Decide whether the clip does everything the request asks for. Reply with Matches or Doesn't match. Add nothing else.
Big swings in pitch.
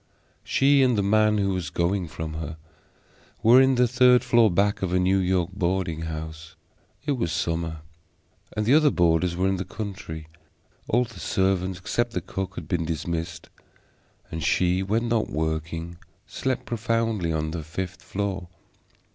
Doesn't match